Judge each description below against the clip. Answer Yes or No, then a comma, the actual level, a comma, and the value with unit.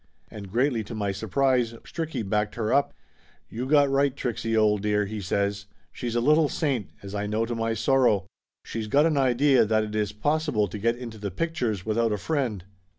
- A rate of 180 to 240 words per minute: Yes, average, 200 wpm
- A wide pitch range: No, average, 4.2 semitones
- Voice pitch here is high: No, low, 115 Hz